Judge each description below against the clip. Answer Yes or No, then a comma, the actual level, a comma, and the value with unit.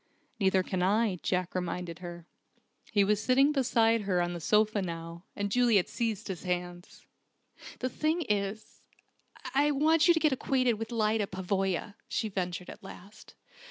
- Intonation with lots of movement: No, average, 4.4 semitones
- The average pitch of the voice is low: No, high, 205 Hz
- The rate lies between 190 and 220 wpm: No, average, 160 wpm